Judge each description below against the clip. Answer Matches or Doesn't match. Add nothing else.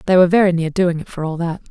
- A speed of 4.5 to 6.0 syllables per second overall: Doesn't match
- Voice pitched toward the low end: Doesn't match